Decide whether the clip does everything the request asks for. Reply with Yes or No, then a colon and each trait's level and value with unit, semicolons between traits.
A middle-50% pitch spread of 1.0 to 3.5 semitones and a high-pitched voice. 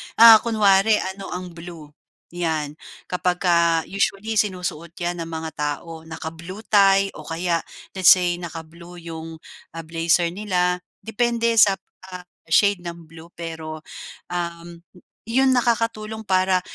No: average, 3.1 semitones; medium, 175 Hz